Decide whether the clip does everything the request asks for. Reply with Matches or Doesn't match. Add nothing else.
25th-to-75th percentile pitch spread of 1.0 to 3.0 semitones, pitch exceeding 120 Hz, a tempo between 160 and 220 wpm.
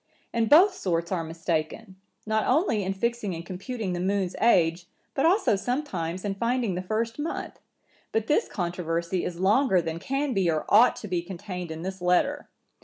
Doesn't match